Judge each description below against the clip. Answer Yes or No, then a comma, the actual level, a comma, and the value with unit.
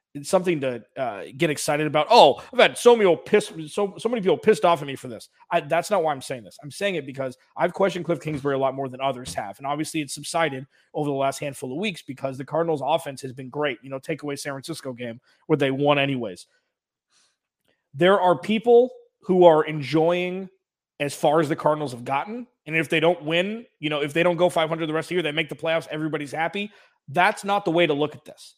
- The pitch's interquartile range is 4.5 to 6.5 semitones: No, average, 3.9 semitones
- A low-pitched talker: No, medium, 155 Hz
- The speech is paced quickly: Yes, fast, 245 wpm